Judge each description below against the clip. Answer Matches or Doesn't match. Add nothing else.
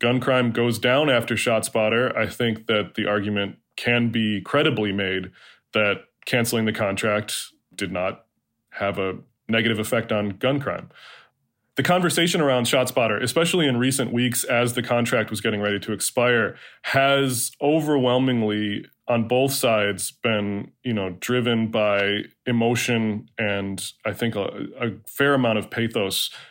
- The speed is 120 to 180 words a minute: Matches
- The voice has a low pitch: Matches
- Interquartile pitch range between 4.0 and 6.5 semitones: Doesn't match